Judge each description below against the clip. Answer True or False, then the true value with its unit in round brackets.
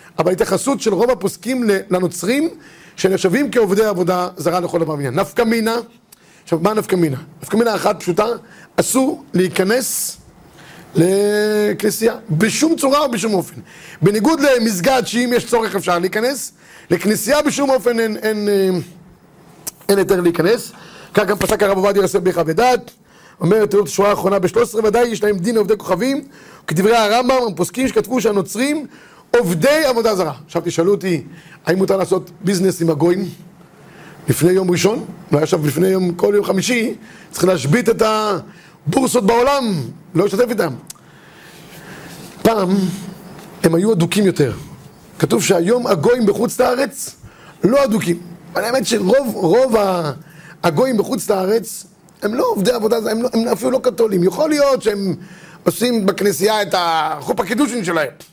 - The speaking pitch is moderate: False (200 Hz)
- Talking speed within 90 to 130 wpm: False (140 wpm)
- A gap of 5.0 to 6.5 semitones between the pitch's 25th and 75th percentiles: False (4.6 semitones)